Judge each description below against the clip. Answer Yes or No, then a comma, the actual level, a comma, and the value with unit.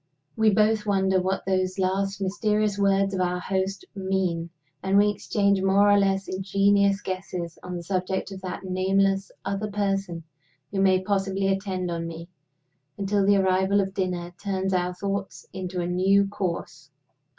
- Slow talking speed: No, average, 160 wpm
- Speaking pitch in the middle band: No, high, 195 Hz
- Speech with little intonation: Yes, narrow, 1.2 semitones